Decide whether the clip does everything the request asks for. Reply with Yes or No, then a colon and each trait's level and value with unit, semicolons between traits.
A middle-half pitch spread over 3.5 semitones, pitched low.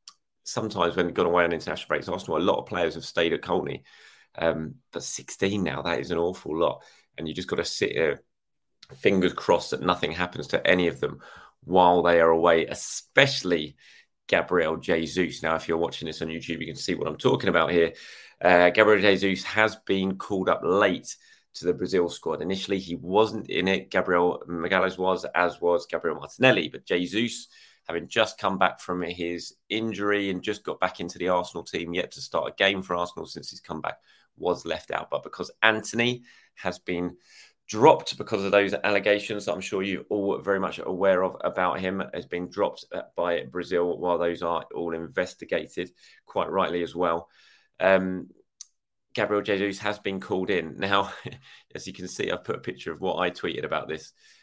No: average, 2.7 semitones; very low, 90 Hz